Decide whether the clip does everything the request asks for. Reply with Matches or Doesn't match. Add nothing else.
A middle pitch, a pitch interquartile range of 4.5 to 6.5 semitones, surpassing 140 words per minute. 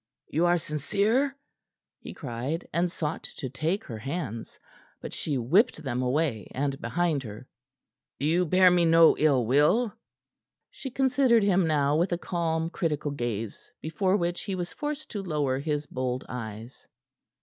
Matches